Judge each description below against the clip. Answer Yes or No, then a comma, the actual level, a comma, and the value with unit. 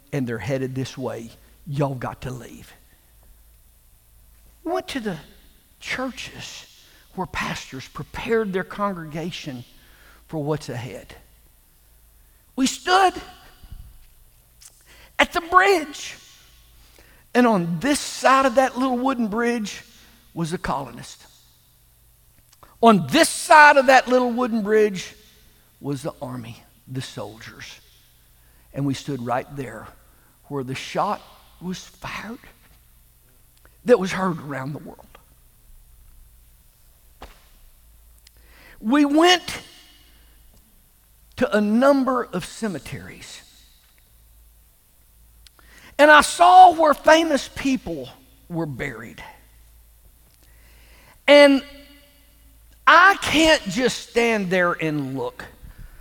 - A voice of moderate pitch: Yes, medium, 165 Hz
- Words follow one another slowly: Yes, slow, 95 wpm